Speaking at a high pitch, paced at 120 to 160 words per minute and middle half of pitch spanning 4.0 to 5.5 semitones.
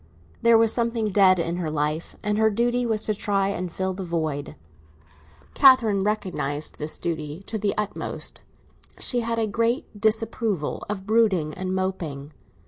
Yes: high, 200 Hz; average, 155 wpm; average, 4.7 semitones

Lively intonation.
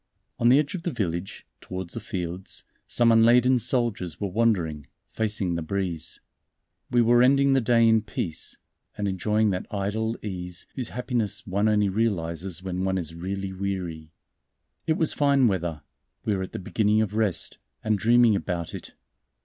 No: average, 4.1 semitones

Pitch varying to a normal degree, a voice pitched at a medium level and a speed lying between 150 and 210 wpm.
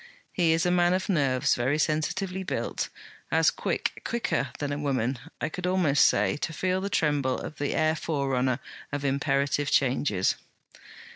Yes: average, 4.3 semitones; medium, 145 Hz; average, 160 wpm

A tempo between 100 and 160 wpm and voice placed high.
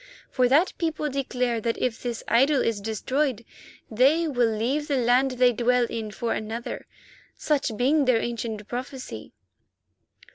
Yes: average, 145 wpm; high, 245 Hz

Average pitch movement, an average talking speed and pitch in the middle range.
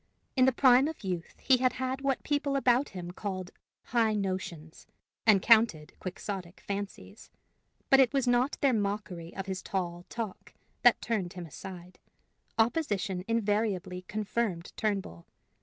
No: average, 4.9 semitones; average, 145 wpm; high, 205 Hz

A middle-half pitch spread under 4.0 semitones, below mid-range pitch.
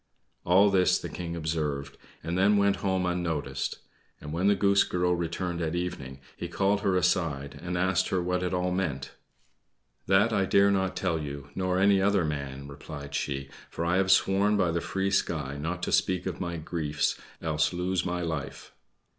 Yes: average, 3.5 semitones; very low, 90 Hz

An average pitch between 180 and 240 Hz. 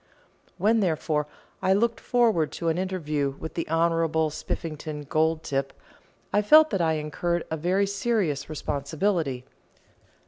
No: medium, 165 Hz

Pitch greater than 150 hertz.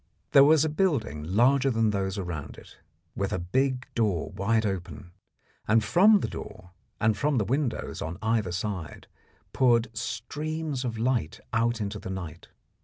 No: low, 110 Hz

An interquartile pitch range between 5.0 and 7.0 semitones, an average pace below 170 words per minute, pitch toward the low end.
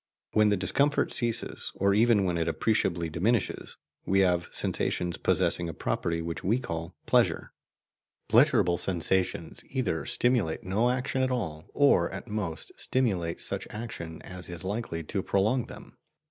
Yes: wide, 5.6 semitones; average, 145 wpm; very low, 95 Hz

